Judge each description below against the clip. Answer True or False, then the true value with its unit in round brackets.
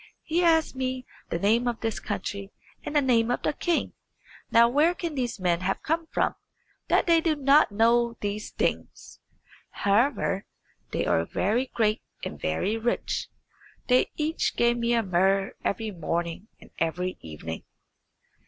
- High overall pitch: True (230 Hz)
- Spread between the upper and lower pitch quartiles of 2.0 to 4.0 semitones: False (5.4 semitones)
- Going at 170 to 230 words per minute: False (155 wpm)